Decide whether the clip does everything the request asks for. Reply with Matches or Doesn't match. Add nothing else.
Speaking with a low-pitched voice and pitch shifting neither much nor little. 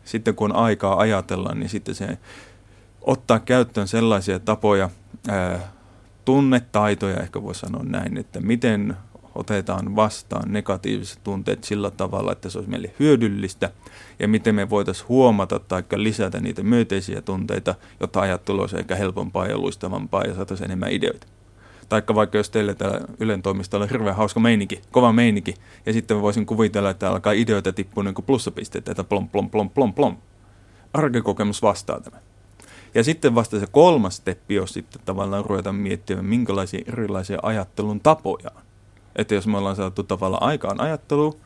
Doesn't match